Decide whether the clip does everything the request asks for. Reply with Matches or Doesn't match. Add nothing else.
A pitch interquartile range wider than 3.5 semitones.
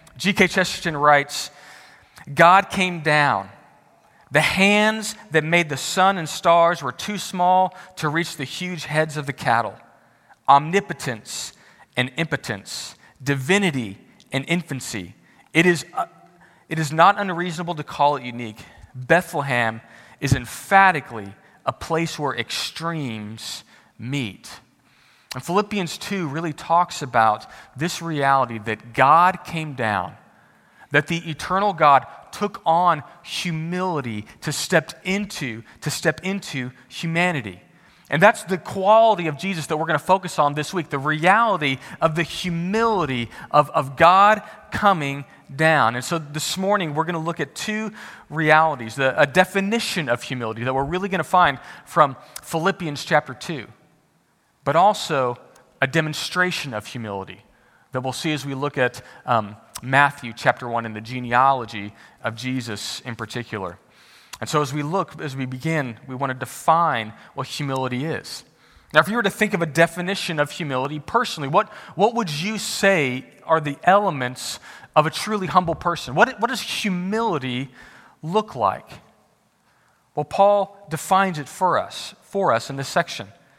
Matches